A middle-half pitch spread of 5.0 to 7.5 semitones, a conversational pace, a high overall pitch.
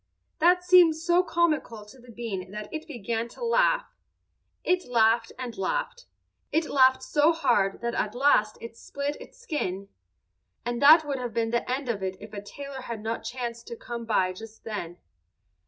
Yes: wide, 5.6 semitones; average, 180 wpm; high, 240 Hz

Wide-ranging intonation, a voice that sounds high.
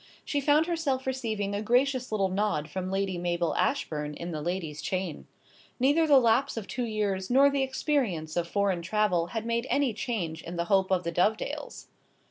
Yes: wide, 6.7 semitones; high, 205 Hz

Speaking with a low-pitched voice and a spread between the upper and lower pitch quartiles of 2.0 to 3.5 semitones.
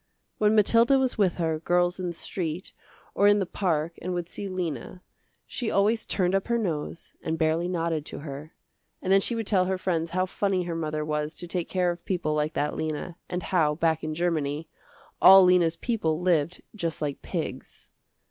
No: medium, 175 Hz; average, 3.1 semitones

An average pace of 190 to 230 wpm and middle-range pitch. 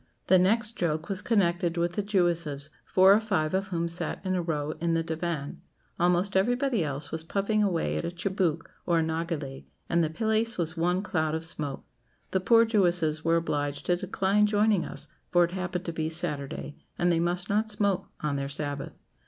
Yes: average, 195 wpm; medium, 175 Hz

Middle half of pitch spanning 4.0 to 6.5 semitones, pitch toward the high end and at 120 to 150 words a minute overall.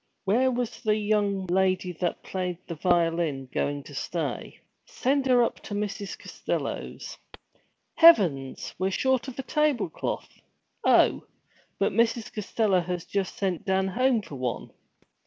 Yes: average, 5.2 semitones; high, 195 Hz; average, 140 wpm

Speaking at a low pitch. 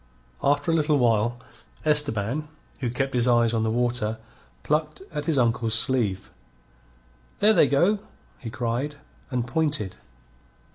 Yes: low, 125 Hz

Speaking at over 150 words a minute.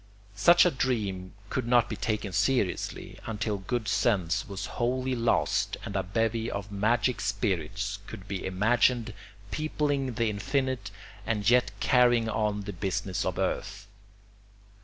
No: average, 140 wpm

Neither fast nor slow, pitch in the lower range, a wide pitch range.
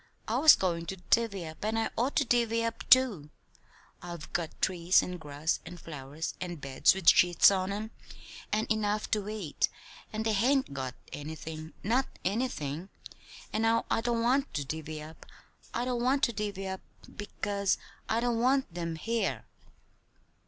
No: average, 165 wpm; high, 200 Hz; wide, 5.9 semitones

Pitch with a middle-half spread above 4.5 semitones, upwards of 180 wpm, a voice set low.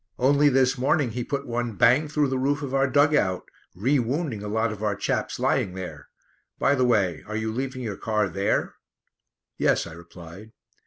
Yes: average, 4.9 semitones; average, 190 wpm; low, 120 Hz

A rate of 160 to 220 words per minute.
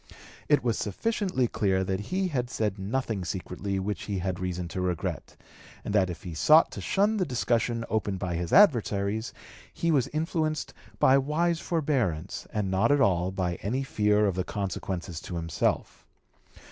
Yes: average, 170 wpm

